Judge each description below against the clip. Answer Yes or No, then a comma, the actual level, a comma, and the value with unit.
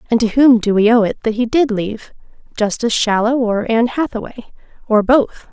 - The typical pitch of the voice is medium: No, high, 230 Hz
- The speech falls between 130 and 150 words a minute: No, average, 185 wpm